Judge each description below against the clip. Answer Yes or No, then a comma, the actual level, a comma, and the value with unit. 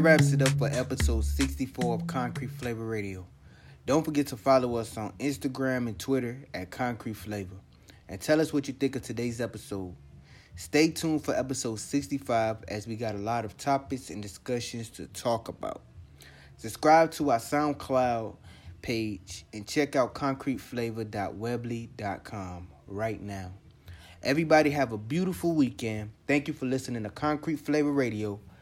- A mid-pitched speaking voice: No, low, 115 Hz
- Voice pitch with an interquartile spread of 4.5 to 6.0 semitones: Yes, wide, 5.6 semitones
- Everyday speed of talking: Yes, average, 150 wpm